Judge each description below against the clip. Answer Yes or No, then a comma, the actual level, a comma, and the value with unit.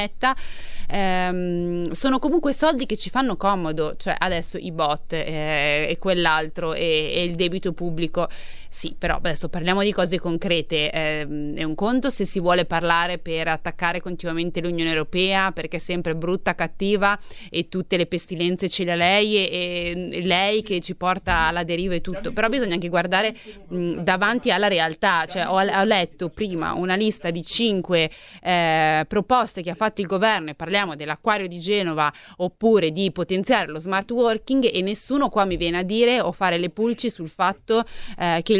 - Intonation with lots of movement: No, average, 3.1 semitones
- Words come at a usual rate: No, fast, 175 wpm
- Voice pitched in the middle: Yes, medium, 180 Hz